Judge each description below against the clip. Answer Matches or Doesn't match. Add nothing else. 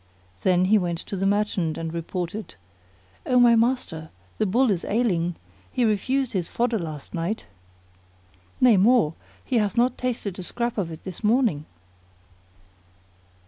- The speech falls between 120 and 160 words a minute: Matches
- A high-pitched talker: Matches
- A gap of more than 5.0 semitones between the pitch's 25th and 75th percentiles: Matches